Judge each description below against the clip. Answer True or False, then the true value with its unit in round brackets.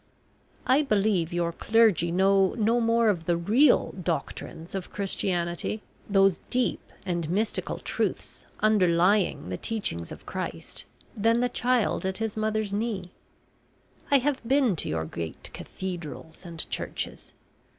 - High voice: True (195 Hz)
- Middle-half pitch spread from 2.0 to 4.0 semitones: False (4.7 semitones)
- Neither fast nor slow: False (130 wpm)